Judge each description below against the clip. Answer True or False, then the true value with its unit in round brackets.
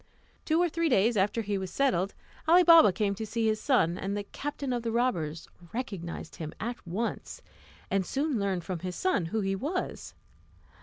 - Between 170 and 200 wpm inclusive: True (190 wpm)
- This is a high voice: True (215 Hz)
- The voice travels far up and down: True (5.9 semitones)